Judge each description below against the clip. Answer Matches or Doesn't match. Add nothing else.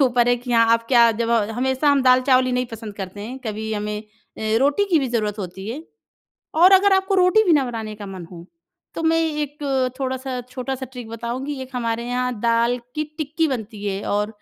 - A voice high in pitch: Matches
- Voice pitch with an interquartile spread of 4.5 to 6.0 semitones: Doesn't match